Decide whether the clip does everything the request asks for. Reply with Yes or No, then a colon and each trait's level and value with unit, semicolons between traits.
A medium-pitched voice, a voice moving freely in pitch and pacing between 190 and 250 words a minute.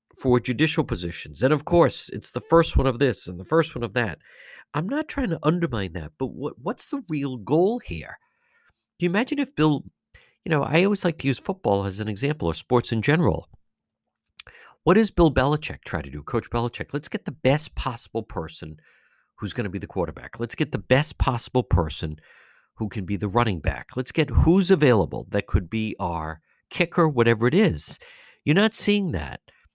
No: low, 130 Hz; wide, 8.5 semitones; average, 200 wpm